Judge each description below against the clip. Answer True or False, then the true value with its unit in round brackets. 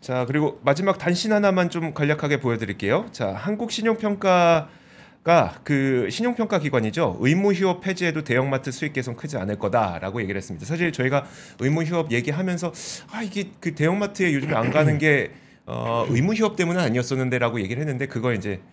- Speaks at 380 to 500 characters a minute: True (405 characters per minute)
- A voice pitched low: False (150 Hz)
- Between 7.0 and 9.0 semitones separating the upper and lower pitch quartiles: False (6.3 semitones)